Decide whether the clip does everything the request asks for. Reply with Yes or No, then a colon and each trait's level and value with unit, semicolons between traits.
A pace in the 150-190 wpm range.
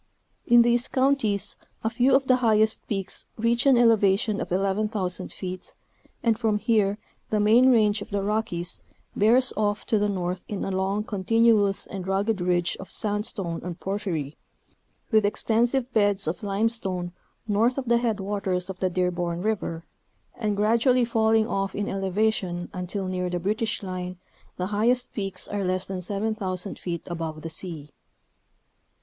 Yes: average, 155 wpm